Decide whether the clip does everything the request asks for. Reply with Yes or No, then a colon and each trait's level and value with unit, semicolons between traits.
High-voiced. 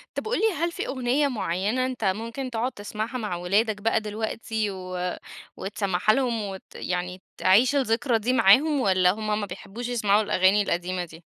Yes: high, 215 Hz